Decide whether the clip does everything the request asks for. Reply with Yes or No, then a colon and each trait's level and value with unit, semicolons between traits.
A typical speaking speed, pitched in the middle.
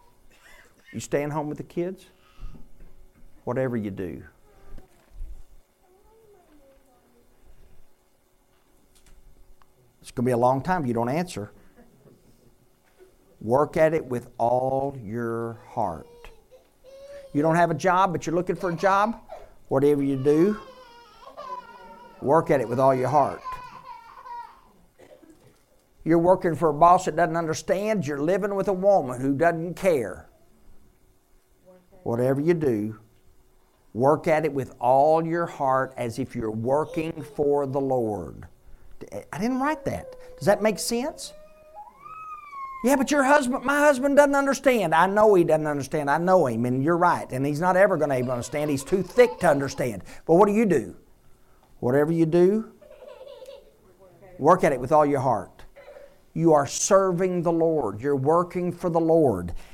Yes: average, 150 wpm; medium, 170 Hz